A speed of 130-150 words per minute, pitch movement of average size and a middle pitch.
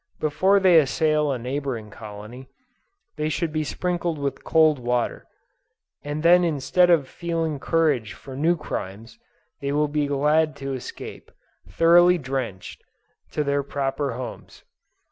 Yes: slow, 135 wpm; average, 3.6 semitones; medium, 145 Hz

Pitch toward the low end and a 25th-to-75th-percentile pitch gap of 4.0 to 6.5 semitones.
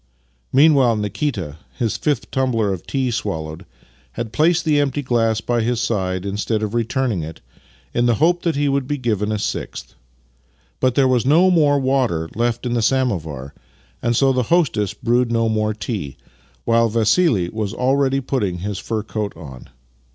Yes: low, 115 Hz; average, 4.4 semitones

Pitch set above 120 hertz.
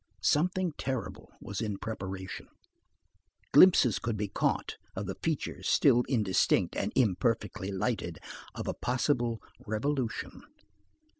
No: low, 115 Hz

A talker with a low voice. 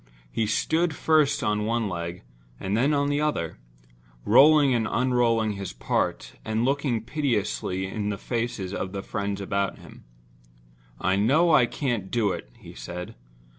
Yes: low, 110 Hz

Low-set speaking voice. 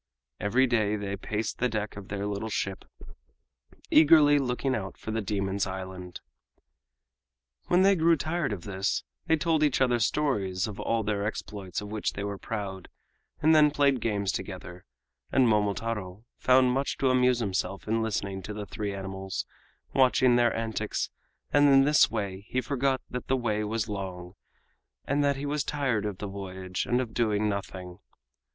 Yes: low, 110 Hz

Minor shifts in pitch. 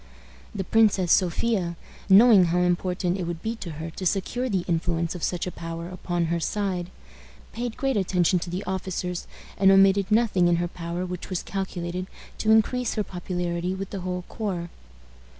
Yes: narrow, 2.3 semitones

